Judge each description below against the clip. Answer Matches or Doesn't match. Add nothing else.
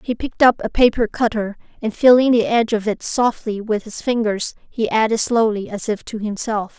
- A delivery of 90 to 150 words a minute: Doesn't match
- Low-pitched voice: Doesn't match